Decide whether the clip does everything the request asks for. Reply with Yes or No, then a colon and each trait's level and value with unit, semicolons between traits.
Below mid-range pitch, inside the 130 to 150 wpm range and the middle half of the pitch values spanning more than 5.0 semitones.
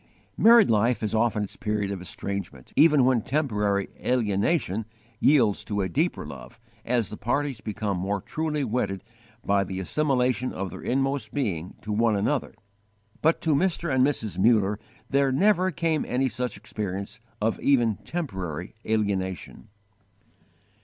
Yes: low, 110 Hz; average, 145 wpm; wide, 5.6 semitones